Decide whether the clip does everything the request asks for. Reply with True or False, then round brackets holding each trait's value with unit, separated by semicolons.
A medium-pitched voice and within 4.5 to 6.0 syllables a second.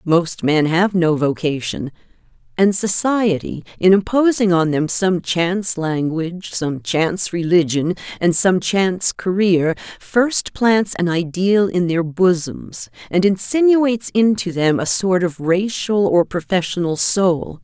False (180 Hz; 3.9 syllables/s)